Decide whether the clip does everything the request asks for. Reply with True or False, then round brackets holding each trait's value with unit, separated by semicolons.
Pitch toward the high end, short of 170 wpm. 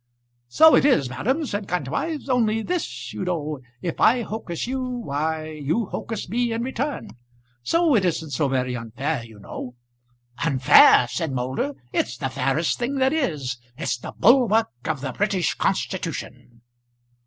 False (165 Hz; 155 wpm)